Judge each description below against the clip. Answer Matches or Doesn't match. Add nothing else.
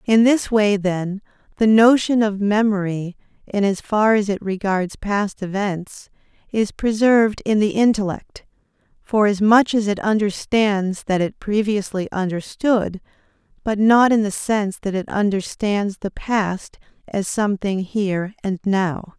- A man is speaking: Doesn't match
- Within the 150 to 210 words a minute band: Doesn't match